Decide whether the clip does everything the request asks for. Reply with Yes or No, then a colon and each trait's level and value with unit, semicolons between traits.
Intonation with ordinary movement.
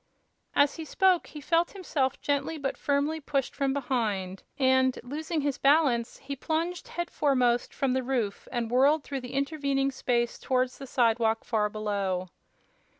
Yes: average, 3.4 semitones